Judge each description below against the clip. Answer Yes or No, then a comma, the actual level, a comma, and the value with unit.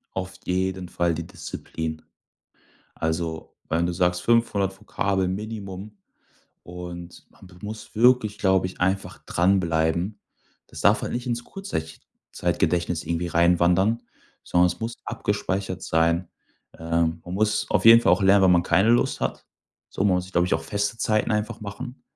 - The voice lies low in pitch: Yes, very low, 95 Hz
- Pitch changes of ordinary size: Yes, average, 3.3 semitones